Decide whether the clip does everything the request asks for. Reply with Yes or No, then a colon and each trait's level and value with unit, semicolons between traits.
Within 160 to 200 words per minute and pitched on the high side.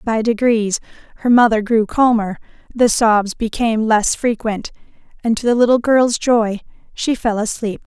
No: average, 150 wpm; high, 225 Hz